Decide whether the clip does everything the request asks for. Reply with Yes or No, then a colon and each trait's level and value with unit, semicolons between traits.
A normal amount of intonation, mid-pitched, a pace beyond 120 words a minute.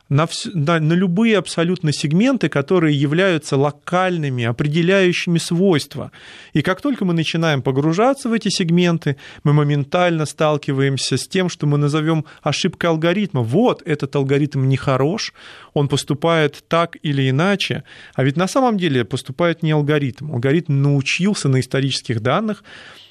Yes: average, 4.0 semitones; medium, 155 Hz; average, 140 wpm